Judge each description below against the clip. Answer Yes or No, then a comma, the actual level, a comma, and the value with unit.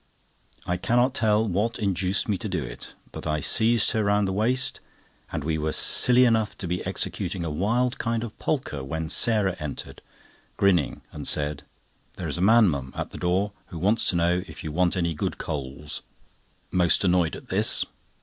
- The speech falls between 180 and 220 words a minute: Yes, average, 190 wpm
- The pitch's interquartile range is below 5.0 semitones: No, wide, 5.4 semitones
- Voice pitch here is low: Yes, very low, 95 Hz